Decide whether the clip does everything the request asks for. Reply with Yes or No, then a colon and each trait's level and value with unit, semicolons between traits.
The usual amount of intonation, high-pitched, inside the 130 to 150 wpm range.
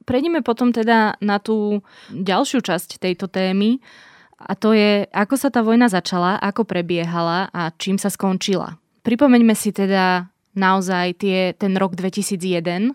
Yes: average, 3.4 semitones; high, 195 Hz; average, 145 wpm